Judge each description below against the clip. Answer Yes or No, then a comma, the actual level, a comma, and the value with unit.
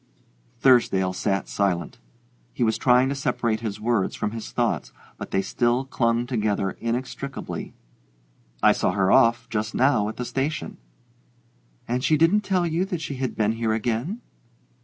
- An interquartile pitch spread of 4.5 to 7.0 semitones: No, average, 3.7 semitones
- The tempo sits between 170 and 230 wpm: No, average, 160 wpm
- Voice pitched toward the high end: No, low, 120 Hz